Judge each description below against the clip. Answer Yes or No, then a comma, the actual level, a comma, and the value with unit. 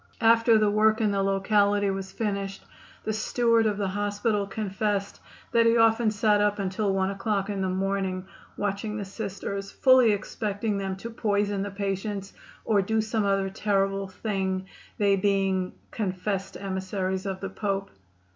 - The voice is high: Yes, high, 200 Hz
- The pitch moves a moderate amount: No, narrow, 1.7 semitones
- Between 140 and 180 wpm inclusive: Yes, average, 155 wpm